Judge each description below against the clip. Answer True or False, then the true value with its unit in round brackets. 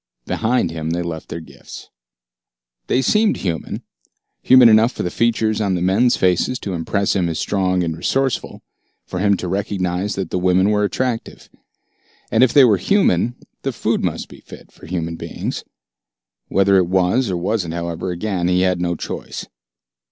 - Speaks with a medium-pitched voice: False (95 Hz)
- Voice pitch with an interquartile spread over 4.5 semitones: False (4.0 semitones)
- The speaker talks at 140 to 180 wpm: True (175 wpm)